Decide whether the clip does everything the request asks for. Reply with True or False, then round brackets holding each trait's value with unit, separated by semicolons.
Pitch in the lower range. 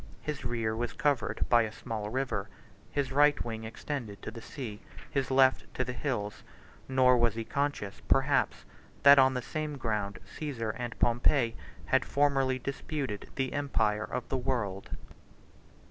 True (125 Hz)